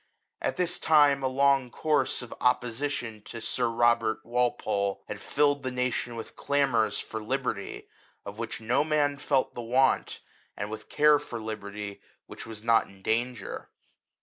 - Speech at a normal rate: Yes, average, 155 wpm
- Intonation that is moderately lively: Yes, average, 3.8 semitones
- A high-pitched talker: No, low, 120 Hz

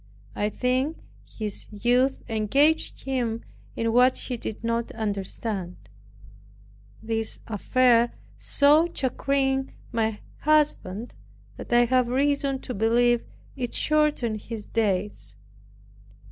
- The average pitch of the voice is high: Yes, high, 240 Hz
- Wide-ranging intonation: No, average, 3.4 semitones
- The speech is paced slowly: Yes, slow, 105 wpm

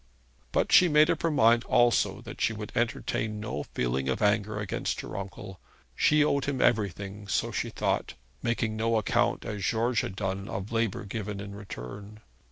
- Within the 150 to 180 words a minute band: Yes, average, 175 wpm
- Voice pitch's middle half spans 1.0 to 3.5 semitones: Yes, average, 2.9 semitones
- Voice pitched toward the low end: Yes, low, 105 Hz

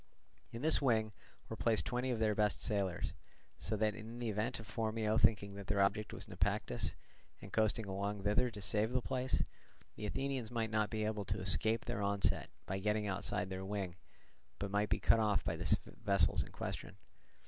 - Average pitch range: No, narrow, 2.0 semitones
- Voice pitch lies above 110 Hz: No, low, 105 Hz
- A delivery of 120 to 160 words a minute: No, average, 190 wpm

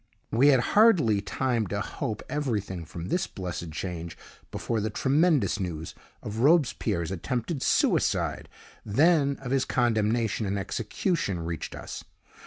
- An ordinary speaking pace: No, slow, 130 wpm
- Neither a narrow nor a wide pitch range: No, wide, 6.0 semitones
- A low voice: Yes, low, 110 Hz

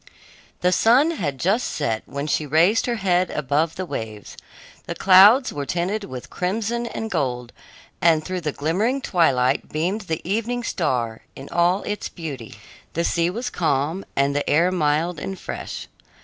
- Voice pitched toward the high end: No, medium, 170 Hz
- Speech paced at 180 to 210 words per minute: No, average, 165 wpm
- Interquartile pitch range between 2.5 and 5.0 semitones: No, wide, 5.5 semitones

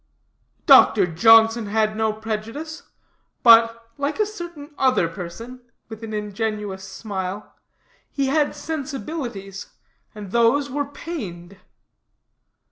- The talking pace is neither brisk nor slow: No, slow, 105 wpm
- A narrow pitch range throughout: No, wide, 5.4 semitones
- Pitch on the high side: Yes, high, 225 Hz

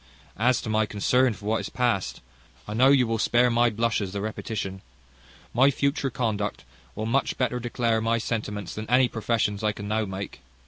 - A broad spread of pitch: No, average, 2.7 semitones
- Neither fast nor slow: Yes, average, 185 wpm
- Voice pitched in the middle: No, low, 115 Hz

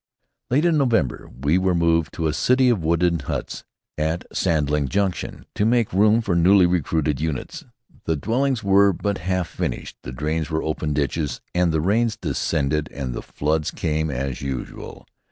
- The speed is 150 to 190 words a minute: Yes, average, 170 wpm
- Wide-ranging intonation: No, average, 4.8 semitones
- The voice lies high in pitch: No, very low, 85 Hz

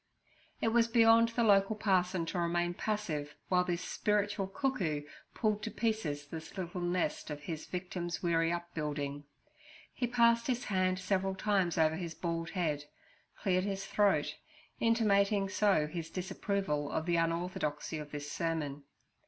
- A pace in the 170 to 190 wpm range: No, average, 145 wpm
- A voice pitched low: No, medium, 180 Hz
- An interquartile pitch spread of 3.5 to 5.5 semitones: Yes, average, 4.1 semitones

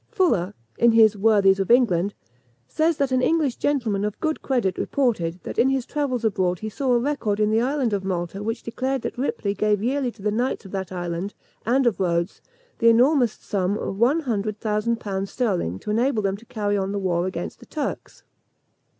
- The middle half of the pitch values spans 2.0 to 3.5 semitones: No, average, 4.5 semitones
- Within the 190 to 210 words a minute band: Yes, average, 200 wpm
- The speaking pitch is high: Yes, high, 215 Hz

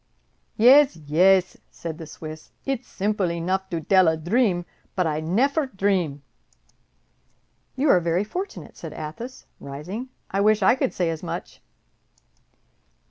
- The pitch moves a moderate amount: No, wide, 5.7 semitones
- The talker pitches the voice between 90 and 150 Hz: No, medium, 185 Hz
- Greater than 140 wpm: No, slow, 135 wpm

